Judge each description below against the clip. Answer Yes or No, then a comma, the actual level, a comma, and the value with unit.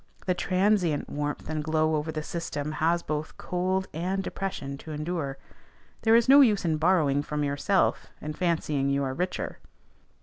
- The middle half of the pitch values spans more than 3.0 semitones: Yes, average, 3.7 semitones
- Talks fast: No, average, 165 wpm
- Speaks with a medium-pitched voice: Yes, medium, 160 Hz